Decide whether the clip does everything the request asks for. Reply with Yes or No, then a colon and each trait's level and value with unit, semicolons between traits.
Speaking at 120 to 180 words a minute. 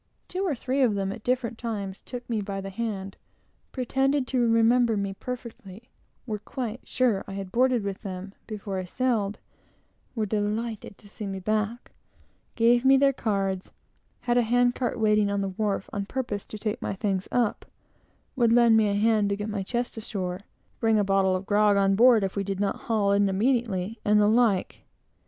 No: average, 190 wpm